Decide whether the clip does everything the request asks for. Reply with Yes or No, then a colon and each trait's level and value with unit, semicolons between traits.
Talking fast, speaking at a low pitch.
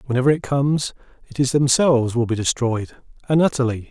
No: average, 170 wpm; low, 130 Hz